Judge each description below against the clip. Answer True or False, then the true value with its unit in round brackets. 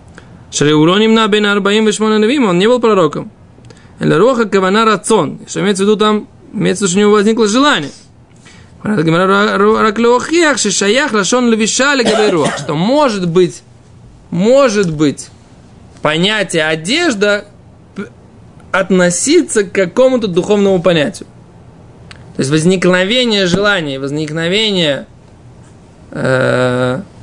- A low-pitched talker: False (205 Hz)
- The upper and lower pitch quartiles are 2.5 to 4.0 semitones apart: True (3.7 semitones)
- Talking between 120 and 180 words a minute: False (110 wpm)